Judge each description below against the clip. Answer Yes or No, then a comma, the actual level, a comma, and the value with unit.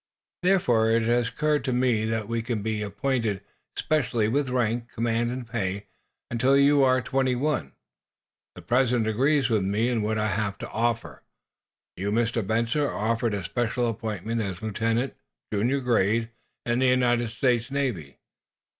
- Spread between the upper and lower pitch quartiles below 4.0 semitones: Yes, narrow, 2.6 semitones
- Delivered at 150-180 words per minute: Yes, average, 160 wpm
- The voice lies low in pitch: Yes, low, 115 Hz